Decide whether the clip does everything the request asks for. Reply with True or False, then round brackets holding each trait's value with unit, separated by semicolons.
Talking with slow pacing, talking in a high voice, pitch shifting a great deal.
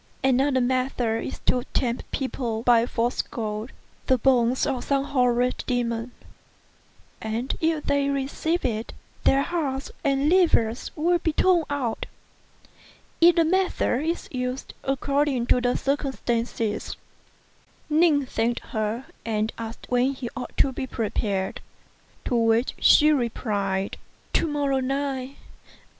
False (120 wpm; 255 Hz; 3.3 semitones)